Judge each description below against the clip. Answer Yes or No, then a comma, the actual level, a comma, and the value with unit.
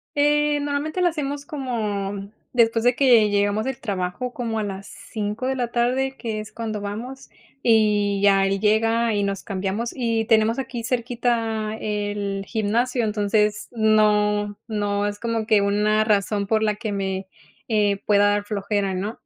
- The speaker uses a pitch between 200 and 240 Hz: Yes, high, 215 Hz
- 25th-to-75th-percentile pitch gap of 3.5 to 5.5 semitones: No, narrow, 2.6 semitones